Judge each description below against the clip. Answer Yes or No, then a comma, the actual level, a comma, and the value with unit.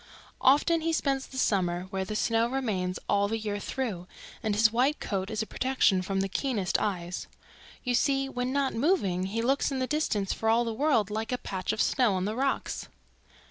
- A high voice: Yes, high, 225 Hz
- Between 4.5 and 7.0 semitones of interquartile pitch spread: Yes, average, 5.3 semitones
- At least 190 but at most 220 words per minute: Yes, fast, 205 wpm